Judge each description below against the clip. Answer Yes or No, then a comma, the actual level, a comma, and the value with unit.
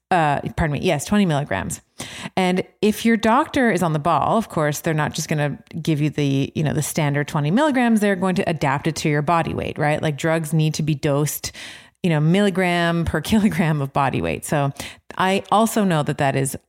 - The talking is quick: Yes, fast, 220 wpm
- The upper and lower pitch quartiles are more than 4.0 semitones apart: Yes, average, 4.4 semitones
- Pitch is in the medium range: Yes, medium, 160 Hz